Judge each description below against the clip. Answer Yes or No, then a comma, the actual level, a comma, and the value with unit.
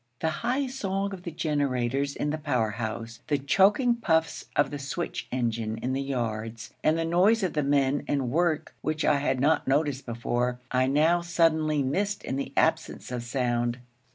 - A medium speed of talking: Yes, average, 180 wpm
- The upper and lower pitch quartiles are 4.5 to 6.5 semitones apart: Yes, average, 4.8 semitones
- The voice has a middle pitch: Yes, medium, 145 Hz